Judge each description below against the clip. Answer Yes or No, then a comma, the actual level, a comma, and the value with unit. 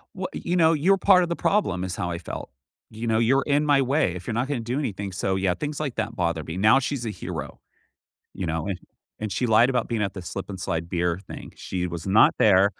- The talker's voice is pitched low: Yes, low, 110 Hz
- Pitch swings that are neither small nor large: No, wide, 6.8 semitones